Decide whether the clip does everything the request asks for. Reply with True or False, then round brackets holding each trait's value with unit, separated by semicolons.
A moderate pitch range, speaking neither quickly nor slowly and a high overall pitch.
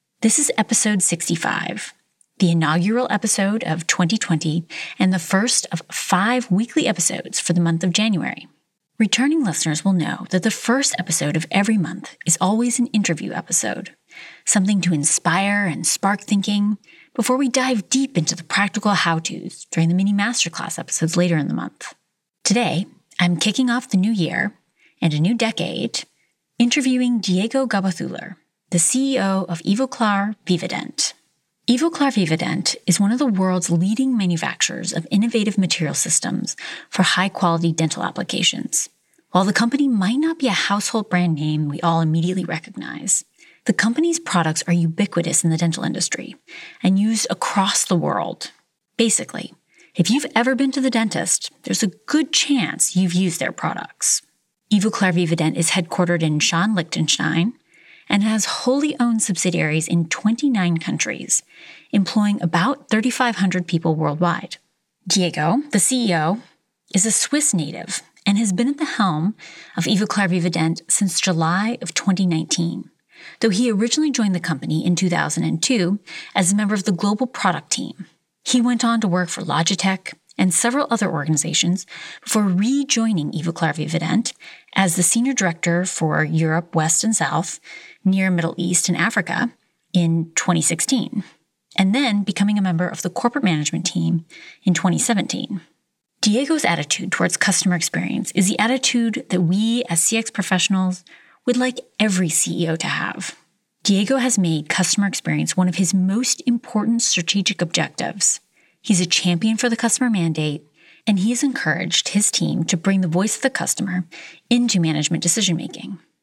True (4.8 semitones; 150 wpm; 195 Hz)